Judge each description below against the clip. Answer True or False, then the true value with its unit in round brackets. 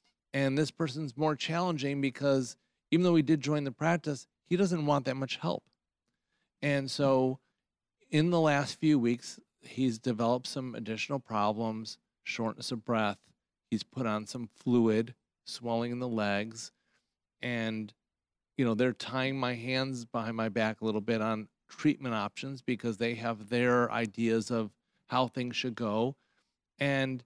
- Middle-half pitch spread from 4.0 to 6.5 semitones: False (3.5 semitones)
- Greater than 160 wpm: False (155 wpm)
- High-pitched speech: False (125 Hz)